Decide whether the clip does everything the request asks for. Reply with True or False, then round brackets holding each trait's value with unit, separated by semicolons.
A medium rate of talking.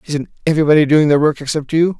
False (210 wpm)